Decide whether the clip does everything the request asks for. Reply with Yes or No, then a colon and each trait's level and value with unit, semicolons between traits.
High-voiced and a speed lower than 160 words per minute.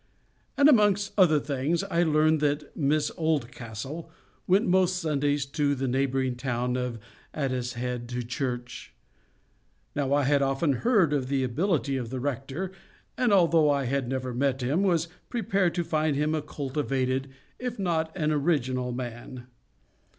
No: medium, 145 Hz; average, 150 wpm